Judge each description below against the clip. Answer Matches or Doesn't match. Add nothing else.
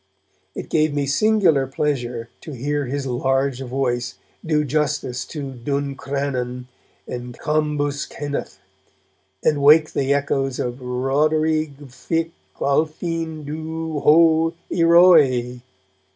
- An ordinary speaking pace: Doesn't match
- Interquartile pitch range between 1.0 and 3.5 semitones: Matches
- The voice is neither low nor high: Matches